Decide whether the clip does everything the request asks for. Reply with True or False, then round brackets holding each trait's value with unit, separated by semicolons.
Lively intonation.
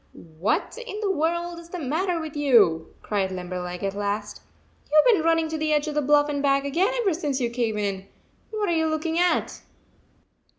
True (8.1 semitones)